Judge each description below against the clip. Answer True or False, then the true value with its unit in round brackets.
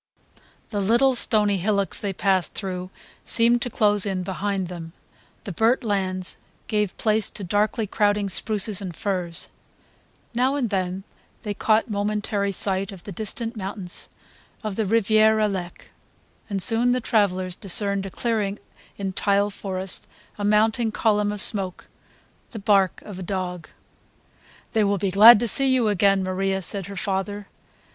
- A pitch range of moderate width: False (2.2 semitones)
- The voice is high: True (200 Hz)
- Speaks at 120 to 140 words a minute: False (150 wpm)